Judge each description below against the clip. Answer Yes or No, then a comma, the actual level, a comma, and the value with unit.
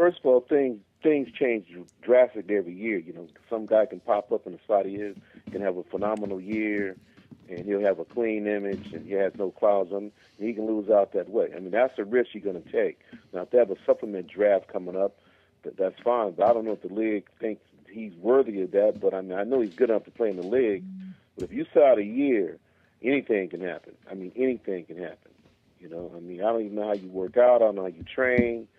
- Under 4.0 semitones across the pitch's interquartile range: No, average, 5.1 semitones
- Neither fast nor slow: No, fast, 255 wpm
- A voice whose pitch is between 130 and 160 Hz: No, low, 110 Hz